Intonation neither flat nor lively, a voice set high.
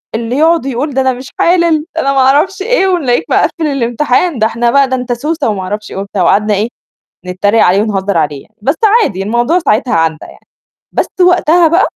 No: wide, 6.9 semitones; very high, 255 Hz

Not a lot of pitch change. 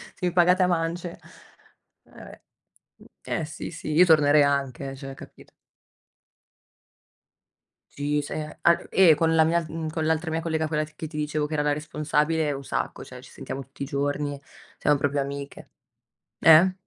Yes: narrow, 2.2 semitones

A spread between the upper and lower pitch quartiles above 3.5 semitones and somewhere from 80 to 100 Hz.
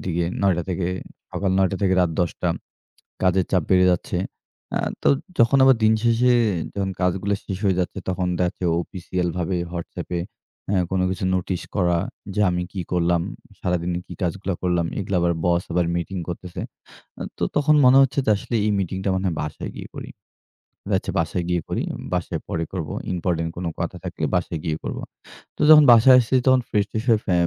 No: narrow, 2.4 semitones; very low, 90 Hz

